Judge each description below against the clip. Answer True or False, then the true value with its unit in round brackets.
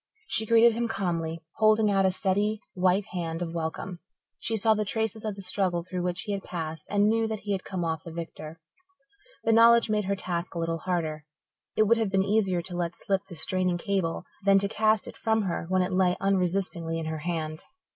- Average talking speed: False (215 wpm)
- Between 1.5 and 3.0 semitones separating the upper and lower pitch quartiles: False (3.6 semitones)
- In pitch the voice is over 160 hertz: True (190 Hz)